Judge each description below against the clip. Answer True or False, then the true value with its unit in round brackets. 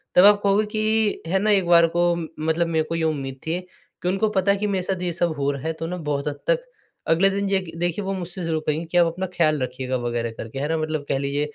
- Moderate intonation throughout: True (3.9 semitones)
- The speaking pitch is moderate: True (170 Hz)